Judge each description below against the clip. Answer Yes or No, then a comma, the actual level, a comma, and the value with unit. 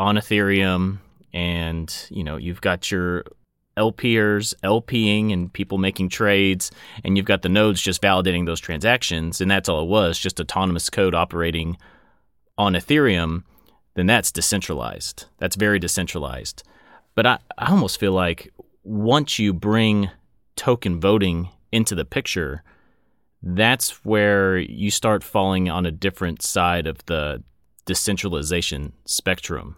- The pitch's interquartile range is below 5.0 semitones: Yes, average, 2.9 semitones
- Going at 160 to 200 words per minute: No, slow, 135 wpm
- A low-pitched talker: Yes, very low, 95 Hz